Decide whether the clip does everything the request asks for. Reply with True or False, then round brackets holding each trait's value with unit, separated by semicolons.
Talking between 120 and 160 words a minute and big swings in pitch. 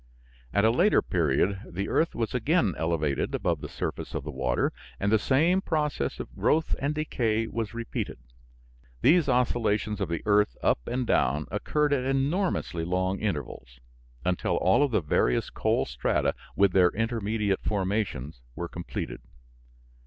True (155 wpm; 7.1 semitones)